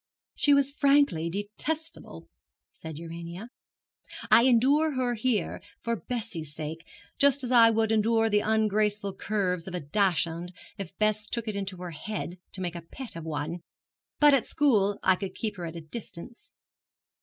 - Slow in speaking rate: No, average, 165 wpm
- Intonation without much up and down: No, average, 5.3 semitones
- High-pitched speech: Yes, high, 210 Hz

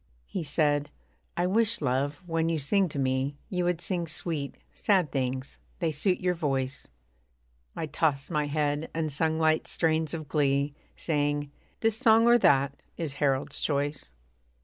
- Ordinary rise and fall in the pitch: Yes, average, 3.2 semitones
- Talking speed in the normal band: Yes, average, 155 wpm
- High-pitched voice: No, medium, 150 Hz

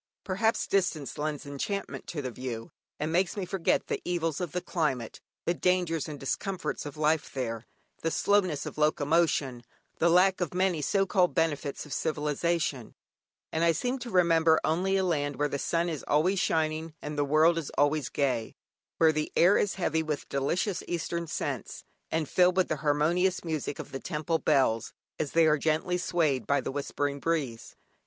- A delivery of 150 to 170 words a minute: No, average, 180 wpm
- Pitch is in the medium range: Yes, medium, 160 Hz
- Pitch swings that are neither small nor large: Yes, average, 3.5 semitones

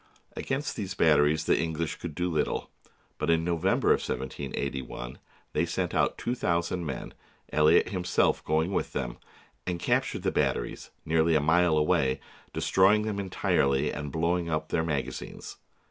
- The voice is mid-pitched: No, very low, 80 Hz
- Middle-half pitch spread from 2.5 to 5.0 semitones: Yes, average, 2.9 semitones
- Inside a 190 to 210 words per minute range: No, average, 155 wpm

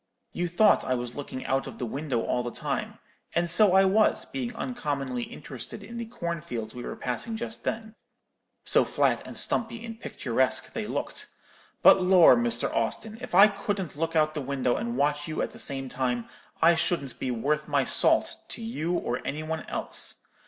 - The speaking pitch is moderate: Yes, medium, 155 Hz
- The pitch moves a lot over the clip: Yes, wide, 7.9 semitones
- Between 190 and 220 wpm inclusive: Yes, average, 195 wpm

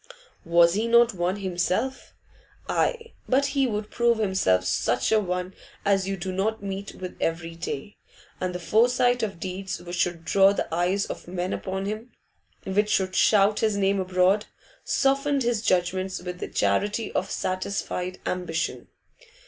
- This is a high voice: Yes, high, 195 Hz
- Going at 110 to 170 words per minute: Yes, average, 155 wpm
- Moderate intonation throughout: Yes, average, 3.1 semitones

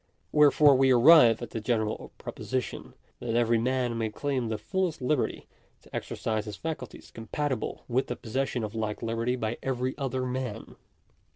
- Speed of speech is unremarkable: Yes, average, 170 wpm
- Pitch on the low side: Yes, low, 125 Hz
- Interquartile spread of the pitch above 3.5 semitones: No, average, 2.9 semitones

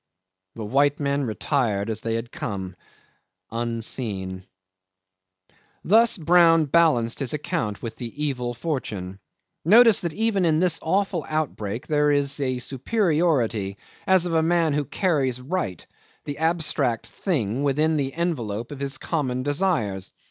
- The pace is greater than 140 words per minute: No, slow, 135 wpm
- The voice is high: No, medium, 140 Hz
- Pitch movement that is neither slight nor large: No, wide, 6.2 semitones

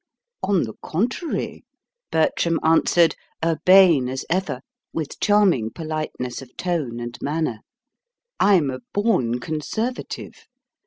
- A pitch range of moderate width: No, wide, 6.4 semitones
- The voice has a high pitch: No, medium, 160 Hz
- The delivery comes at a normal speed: No, slow, 105 wpm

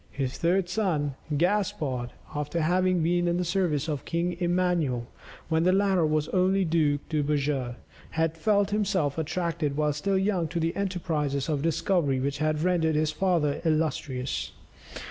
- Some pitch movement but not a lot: Yes, average, 3.6 semitones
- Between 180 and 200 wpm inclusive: No, average, 155 wpm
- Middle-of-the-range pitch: Yes, medium, 165 Hz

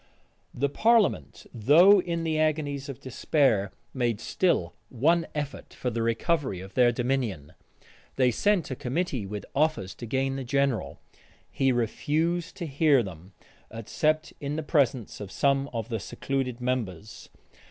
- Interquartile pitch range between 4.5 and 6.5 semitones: Yes, average, 5.2 semitones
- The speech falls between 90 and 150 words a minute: Yes, average, 145 wpm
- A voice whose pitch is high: No, low, 135 Hz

